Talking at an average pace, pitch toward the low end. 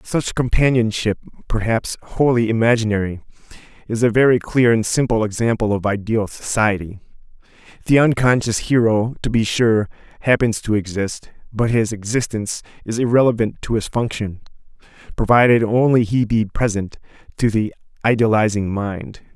No: slow, 125 wpm; low, 110 Hz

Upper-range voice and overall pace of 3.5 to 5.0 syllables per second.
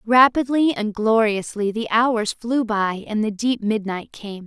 Yes: high, 220 Hz; 4.0 syllables/s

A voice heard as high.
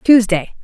Yes: high, 210 Hz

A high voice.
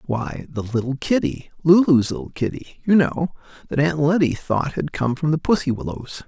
No: medium, 145 Hz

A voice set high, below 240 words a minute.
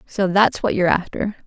Yes: high, 195 Hz; fast, 205 wpm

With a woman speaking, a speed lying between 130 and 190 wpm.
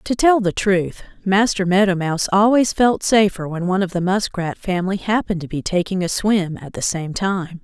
No: female; fast, 205 wpm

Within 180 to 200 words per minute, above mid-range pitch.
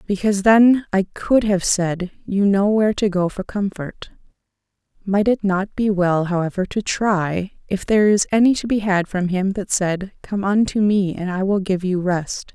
Yes: average, 190 wpm; high, 195 Hz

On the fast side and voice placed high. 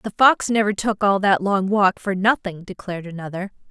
No: average, 195 wpm; high, 195 Hz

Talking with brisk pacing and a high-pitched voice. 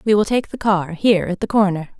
Yes: fast, 270 wpm; high, 200 Hz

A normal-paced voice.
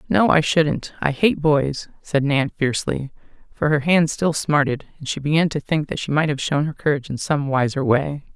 No: fast, 215 wpm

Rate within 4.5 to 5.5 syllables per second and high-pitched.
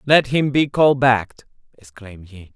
No: 5.1 syllables/s; low, 120 Hz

